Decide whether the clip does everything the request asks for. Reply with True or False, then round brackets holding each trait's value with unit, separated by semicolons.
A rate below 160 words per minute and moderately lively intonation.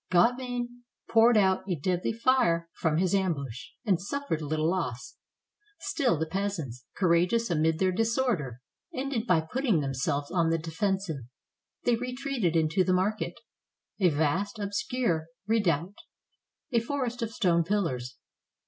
False (140 wpm; 6.1 semitones)